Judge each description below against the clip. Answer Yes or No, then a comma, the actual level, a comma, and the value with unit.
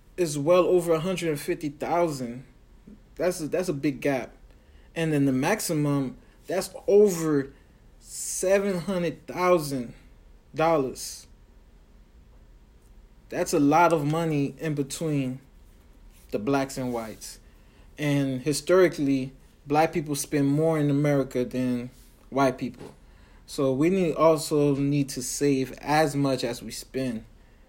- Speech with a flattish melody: No, average, 3.8 semitones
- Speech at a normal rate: No, slow, 115 wpm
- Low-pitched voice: No, medium, 145 Hz